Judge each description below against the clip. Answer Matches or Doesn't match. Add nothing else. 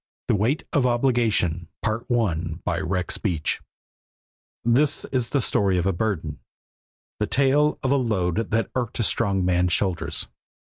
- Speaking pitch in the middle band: Doesn't match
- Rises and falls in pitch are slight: Doesn't match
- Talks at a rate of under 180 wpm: Matches